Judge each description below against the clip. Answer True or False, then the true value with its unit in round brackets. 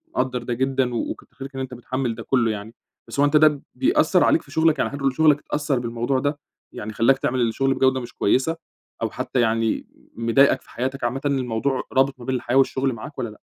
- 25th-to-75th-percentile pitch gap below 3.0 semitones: True (2.6 semitones)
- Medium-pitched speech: False (130 Hz)